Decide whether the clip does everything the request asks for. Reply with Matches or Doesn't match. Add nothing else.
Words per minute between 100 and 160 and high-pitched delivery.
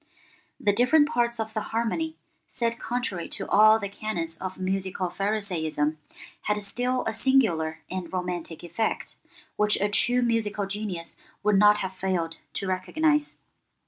Matches